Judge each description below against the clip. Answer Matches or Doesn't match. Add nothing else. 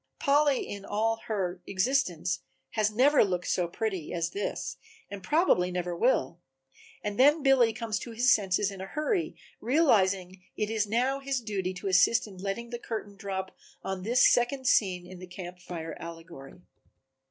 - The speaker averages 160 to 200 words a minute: Matches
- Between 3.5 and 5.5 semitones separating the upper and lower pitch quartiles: Matches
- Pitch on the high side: Matches